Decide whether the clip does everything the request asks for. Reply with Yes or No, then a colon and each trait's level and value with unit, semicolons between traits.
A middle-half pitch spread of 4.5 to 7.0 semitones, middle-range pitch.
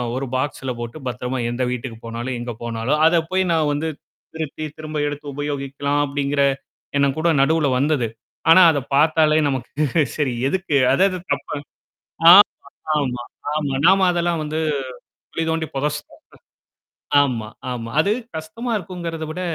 No: average, 3.3 semitones; medium, 145 Hz